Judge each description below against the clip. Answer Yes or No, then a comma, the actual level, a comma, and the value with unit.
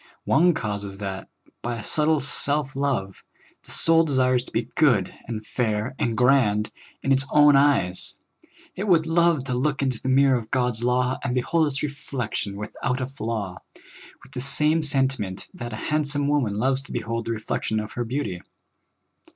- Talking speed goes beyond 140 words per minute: Yes, average, 190 wpm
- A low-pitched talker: Yes, low, 130 Hz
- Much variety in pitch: No, average, 4.4 semitones